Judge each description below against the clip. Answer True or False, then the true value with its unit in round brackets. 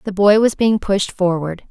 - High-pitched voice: True (195 Hz)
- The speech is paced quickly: True (210 wpm)